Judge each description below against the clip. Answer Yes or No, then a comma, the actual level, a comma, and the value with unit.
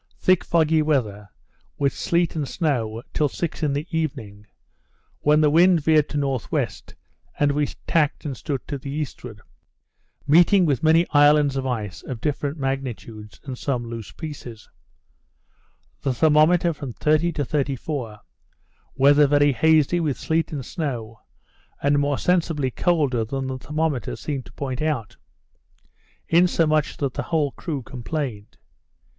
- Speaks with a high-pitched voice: No, medium, 145 Hz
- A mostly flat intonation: No, average, 3.4 semitones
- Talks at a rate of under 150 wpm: Yes, average, 140 wpm